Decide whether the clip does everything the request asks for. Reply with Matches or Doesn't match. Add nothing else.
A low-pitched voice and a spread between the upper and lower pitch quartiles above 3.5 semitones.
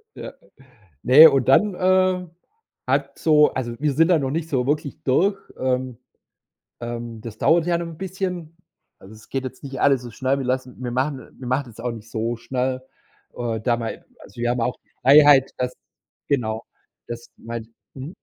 Matches